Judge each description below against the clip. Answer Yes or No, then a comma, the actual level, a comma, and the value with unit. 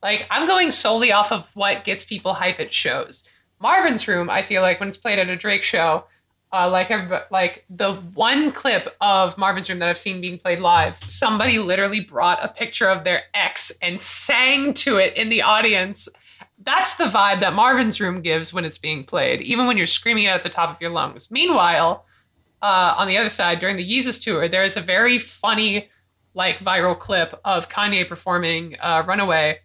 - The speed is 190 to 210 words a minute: Yes, average, 200 wpm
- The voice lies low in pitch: No, high, 195 Hz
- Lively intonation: No, average, 3.8 semitones